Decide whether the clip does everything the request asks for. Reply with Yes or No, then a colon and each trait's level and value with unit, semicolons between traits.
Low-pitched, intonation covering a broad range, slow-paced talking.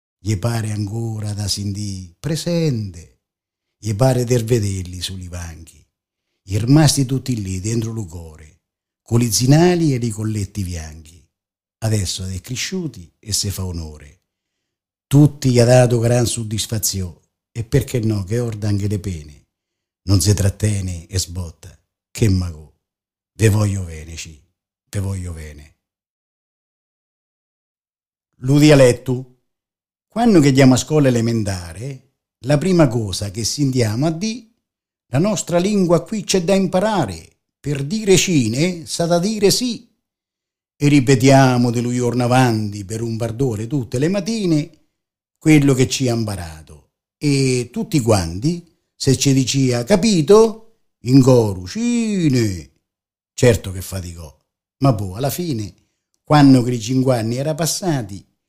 No: low, 115 Hz; wide, 6.5 semitones; average, 135 wpm